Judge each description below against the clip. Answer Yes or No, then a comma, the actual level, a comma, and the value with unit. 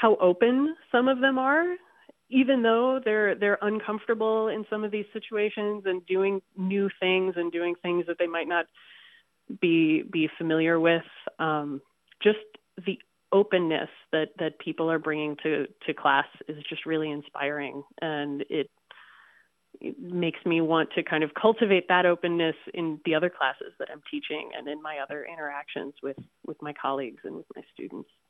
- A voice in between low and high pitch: Yes, medium, 175 Hz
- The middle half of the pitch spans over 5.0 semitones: Yes, wide, 5.4 semitones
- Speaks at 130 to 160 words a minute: No, average, 170 wpm